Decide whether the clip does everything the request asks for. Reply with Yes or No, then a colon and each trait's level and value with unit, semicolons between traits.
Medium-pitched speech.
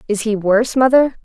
No: high, 230 Hz